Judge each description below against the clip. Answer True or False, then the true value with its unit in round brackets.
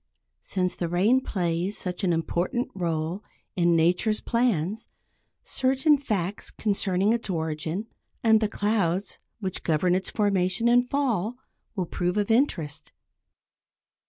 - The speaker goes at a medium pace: False (125 wpm)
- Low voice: False (190 Hz)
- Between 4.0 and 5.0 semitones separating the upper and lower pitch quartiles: True (4.3 semitones)